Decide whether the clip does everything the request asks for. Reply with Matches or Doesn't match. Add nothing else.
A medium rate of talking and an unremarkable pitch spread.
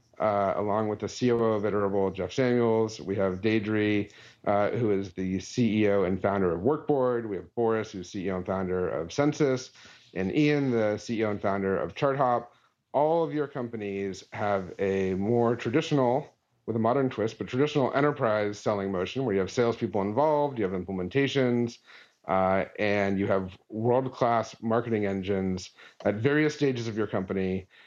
Matches